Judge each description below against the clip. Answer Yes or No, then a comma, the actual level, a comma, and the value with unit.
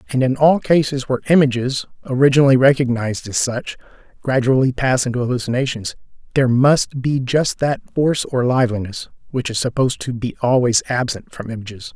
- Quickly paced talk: No, average, 155 wpm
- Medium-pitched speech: No, low, 130 Hz